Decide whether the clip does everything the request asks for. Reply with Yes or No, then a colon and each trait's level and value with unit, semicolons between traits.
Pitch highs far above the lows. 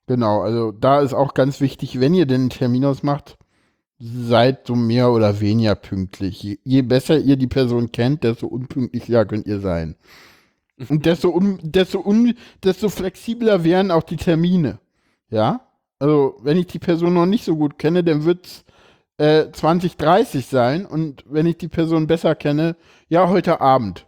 Yes: wide, 5.9 semitones